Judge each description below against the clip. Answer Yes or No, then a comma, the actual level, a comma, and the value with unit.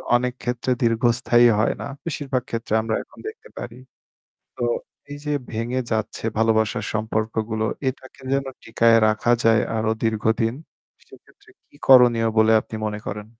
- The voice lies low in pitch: Yes, low, 115 Hz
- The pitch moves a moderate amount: No, narrow, 2.1 semitones